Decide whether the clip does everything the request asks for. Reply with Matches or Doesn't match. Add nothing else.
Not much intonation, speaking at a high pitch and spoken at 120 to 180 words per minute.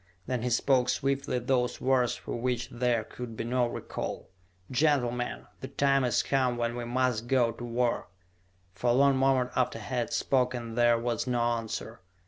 Doesn't match